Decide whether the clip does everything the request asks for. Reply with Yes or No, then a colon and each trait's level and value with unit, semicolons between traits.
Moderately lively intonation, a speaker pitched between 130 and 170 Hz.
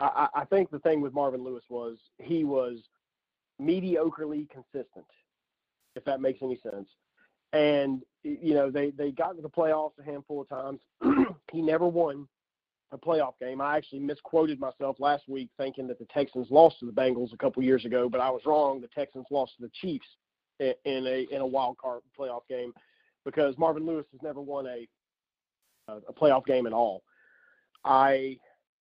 Yes: average, 3.2 semitones; medium, 140 Hz